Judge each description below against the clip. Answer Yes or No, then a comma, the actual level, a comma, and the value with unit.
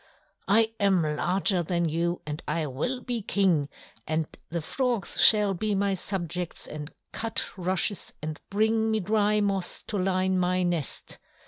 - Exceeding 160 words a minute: No, average, 150 wpm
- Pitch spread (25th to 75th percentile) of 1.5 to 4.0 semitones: Yes, average, 3.6 semitones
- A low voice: No, medium, 185 Hz